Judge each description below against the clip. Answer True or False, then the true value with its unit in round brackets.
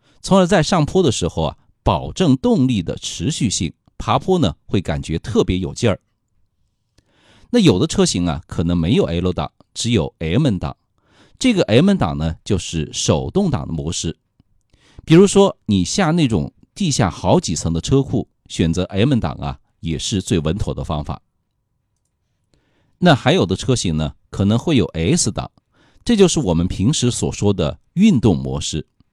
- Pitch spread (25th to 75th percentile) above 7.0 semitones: True (8.1 semitones)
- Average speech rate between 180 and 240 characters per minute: True (230 characters per minute)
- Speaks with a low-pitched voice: True (100 Hz)